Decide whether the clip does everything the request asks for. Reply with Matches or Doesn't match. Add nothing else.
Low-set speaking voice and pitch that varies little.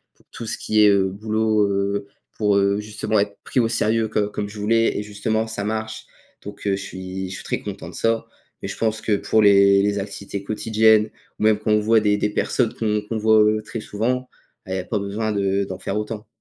Matches